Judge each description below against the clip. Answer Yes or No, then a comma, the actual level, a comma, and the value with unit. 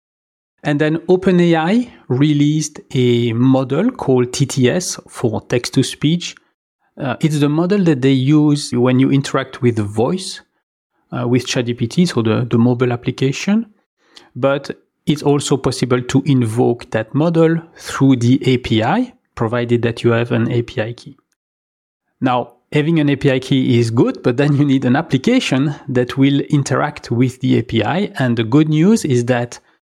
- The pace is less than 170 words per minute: Yes, average, 150 wpm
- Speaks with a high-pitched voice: No, low, 135 Hz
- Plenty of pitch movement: No, average, 3.7 semitones